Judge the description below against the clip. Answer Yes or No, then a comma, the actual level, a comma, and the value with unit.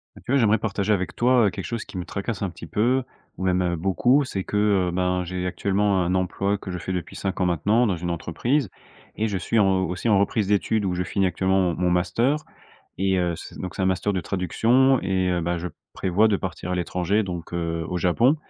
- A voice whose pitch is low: Yes, very low, 95 Hz